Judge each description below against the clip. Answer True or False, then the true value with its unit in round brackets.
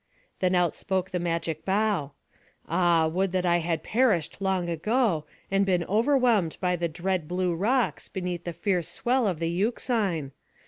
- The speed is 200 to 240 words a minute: False (165 wpm)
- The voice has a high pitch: False (180 Hz)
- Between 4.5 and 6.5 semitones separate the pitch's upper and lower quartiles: False (3.1 semitones)